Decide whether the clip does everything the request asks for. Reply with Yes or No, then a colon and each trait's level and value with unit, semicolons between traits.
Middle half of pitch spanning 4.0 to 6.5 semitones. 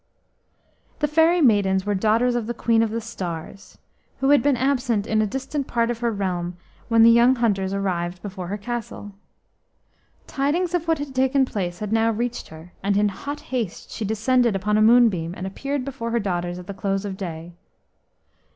Yes: average, 4.5 semitones